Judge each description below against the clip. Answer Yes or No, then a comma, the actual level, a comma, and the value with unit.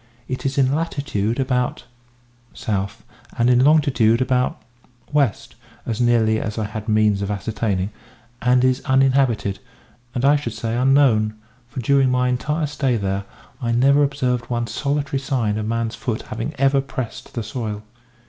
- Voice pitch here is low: Yes, low, 125 Hz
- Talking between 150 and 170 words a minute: Yes, average, 160 wpm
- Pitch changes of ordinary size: Yes, average, 3.7 semitones